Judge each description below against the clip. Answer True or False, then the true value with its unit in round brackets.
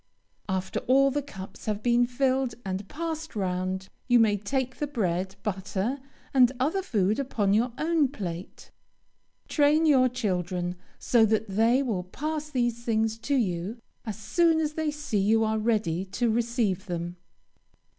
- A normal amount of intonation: False (5.8 semitones)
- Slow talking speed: False (155 wpm)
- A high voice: True (225 Hz)